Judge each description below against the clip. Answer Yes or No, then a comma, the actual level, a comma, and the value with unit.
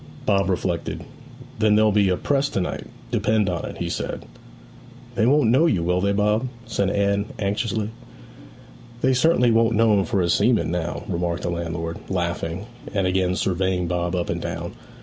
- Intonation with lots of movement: No, average, 3.7 semitones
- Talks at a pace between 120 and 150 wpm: No, average, 175 wpm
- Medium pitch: No, low, 100 Hz